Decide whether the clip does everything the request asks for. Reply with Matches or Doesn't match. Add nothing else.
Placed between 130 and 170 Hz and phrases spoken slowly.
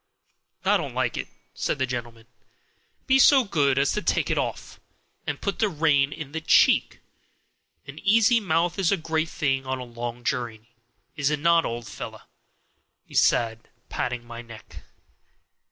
Doesn't match